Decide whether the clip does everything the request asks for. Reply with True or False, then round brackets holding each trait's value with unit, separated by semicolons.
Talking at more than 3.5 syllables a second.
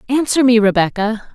True (5.4 syllables/s)